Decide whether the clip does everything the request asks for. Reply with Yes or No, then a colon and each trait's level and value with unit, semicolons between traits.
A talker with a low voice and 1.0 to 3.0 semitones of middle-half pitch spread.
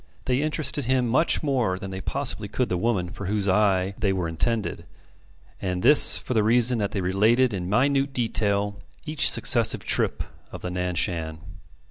No: low, 105 Hz; average, 5.2 semitones